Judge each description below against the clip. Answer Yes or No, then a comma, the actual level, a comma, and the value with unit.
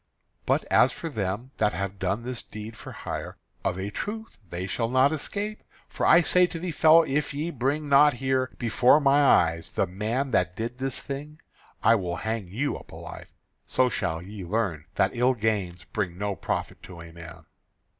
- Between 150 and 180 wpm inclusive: No, average, 190 wpm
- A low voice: Yes, low, 115 Hz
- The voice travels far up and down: Yes, wide, 6.9 semitones